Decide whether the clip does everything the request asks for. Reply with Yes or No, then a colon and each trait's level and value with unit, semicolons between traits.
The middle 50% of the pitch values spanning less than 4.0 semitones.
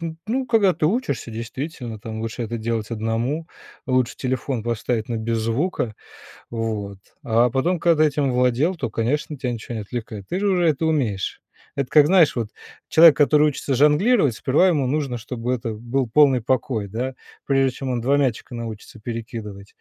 No: average, 4.8 semitones